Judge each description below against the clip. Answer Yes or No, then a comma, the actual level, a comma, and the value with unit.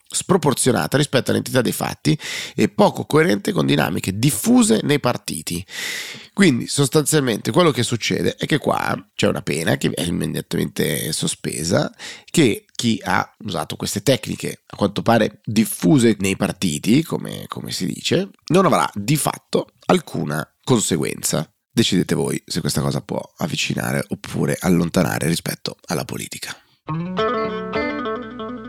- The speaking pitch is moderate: No, low, 120 Hz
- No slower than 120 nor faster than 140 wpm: Yes, average, 130 wpm